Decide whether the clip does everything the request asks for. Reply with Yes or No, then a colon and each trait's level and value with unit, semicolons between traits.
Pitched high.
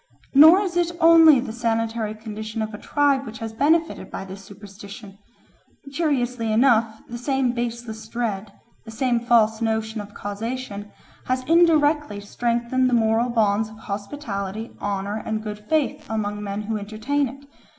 Yes: high, 225 Hz